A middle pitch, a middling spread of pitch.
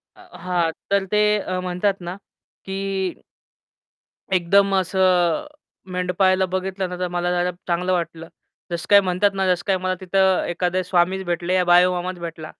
No: medium, 180 Hz; narrow, 1.3 semitones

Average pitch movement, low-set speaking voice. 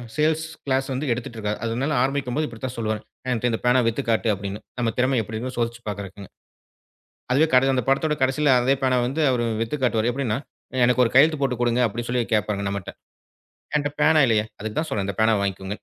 Yes: average, 3.6 semitones; low, 120 Hz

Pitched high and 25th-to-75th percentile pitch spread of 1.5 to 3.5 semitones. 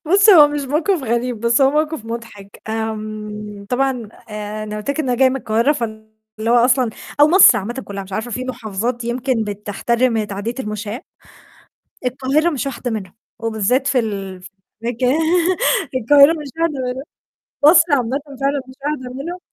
No: high, 240 Hz; average, 4.1 semitones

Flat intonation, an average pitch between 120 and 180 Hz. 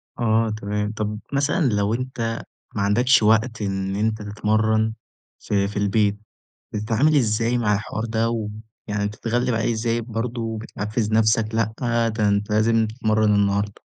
No: narrow, 1.6 semitones; low, 110 Hz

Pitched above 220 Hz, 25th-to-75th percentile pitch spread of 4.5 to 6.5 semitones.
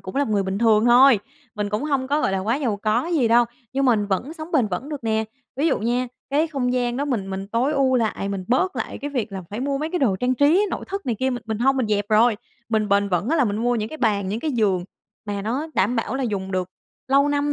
Yes: high, 240 Hz; average, 4.9 semitones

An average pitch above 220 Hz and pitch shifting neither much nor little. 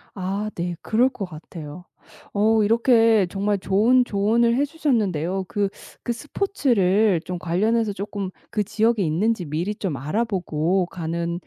No: high, 200 Hz; average, 4.1 semitones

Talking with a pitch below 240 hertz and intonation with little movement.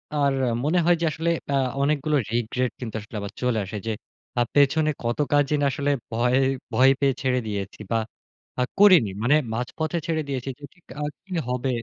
No: low, 135 Hz; average, 4.1 semitones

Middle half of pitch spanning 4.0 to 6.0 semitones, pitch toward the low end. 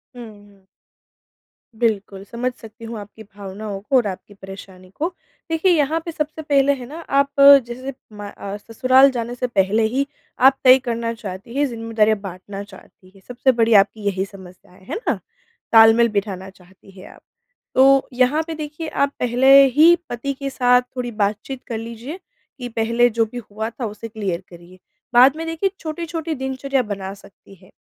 No: average, 4.9 semitones; high, 235 Hz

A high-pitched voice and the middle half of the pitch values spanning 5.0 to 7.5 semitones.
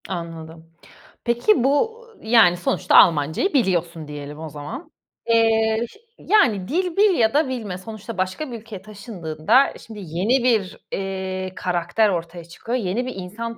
Yes: high, 205 Hz; wide, 5.4 semitones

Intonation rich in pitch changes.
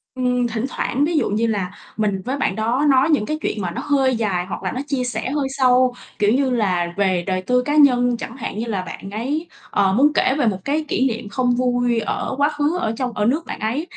No: average, 4.4 semitones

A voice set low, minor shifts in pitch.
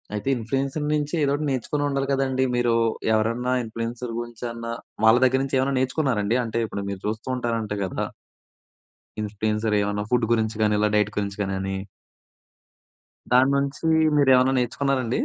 No: low, 120 Hz; average, 3.6 semitones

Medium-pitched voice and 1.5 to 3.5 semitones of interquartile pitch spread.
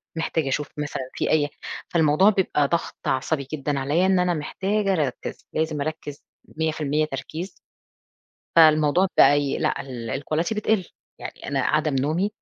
Yes: medium, 155 Hz; average, 3.1 semitones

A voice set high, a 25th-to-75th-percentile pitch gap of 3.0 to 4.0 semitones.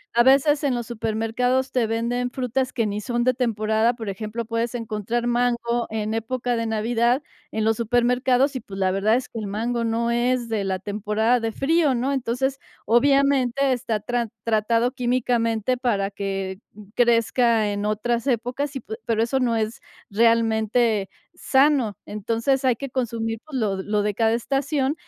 No: high, 235 Hz; narrow, 2.4 semitones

